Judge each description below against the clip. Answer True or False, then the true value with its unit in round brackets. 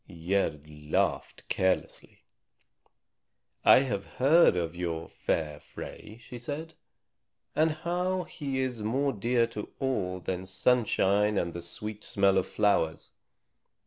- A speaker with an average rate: False (120 wpm)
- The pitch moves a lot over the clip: True (6.5 semitones)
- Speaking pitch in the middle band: False (105 Hz)